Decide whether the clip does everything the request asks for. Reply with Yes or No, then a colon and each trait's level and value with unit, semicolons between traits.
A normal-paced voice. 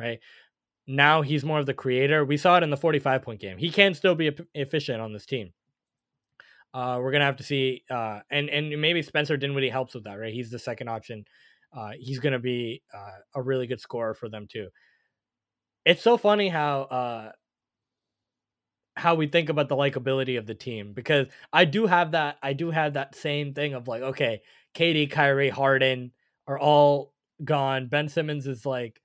Yes: average, 190 wpm